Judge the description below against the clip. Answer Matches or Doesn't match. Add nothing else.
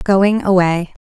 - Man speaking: Doesn't match